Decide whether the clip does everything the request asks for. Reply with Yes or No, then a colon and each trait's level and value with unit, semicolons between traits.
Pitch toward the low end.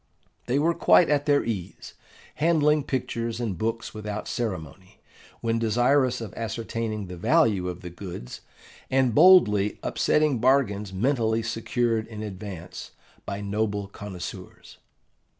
Yes: low, 110 Hz